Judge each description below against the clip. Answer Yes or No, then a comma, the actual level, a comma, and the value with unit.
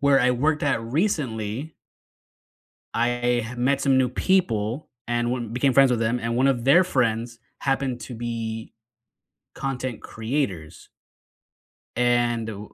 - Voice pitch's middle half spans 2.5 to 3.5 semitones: Yes, average, 2.9 semitones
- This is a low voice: Yes, low, 120 Hz